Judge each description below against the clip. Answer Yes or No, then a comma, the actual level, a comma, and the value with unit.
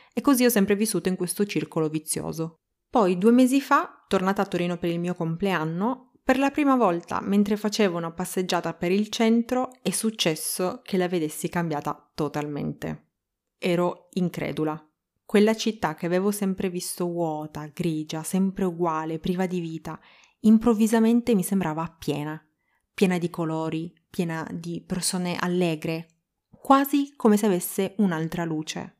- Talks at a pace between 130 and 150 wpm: Yes, average, 145 wpm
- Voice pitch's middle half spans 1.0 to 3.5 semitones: No, average, 4.2 semitones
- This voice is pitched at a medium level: Yes, medium, 180 Hz